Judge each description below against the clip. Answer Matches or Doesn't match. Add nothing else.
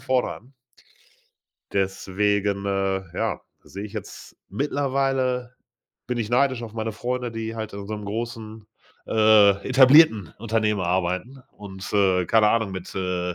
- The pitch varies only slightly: Doesn't match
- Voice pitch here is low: Matches